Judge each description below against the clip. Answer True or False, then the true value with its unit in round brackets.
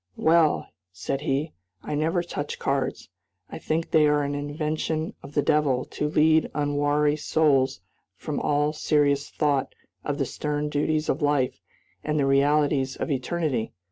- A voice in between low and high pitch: True (150 Hz)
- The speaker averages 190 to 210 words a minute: False (150 wpm)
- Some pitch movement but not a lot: False (1.4 semitones)